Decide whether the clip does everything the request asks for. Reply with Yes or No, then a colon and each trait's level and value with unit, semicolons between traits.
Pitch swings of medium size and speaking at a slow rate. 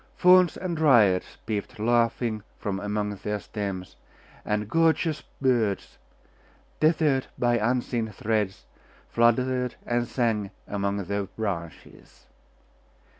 Yes: average, 3.8 semitones; slow, 100 wpm